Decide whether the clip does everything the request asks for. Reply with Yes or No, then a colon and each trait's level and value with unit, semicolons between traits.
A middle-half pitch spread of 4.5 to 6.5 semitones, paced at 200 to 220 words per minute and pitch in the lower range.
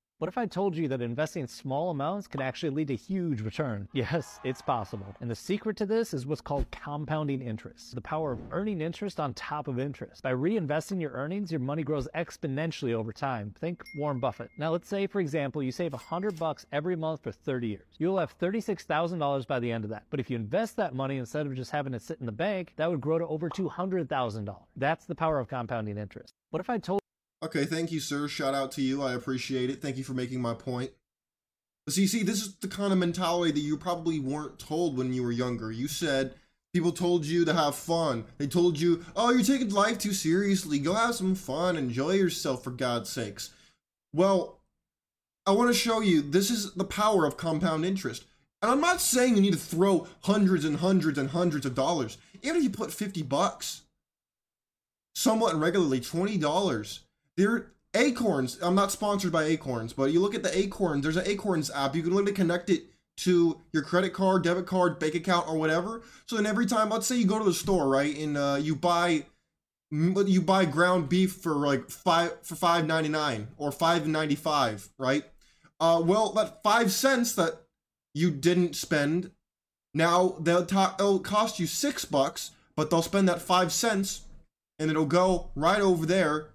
No: average, 5.2 semitones; fast, 205 wpm; medium, 165 Hz